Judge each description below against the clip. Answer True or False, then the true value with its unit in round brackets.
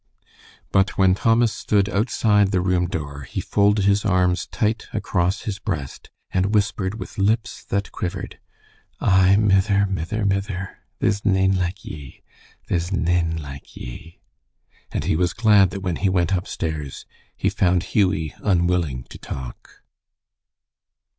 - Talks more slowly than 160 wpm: True (140 wpm)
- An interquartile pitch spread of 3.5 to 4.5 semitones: False (2.5 semitones)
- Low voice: True (95 Hz)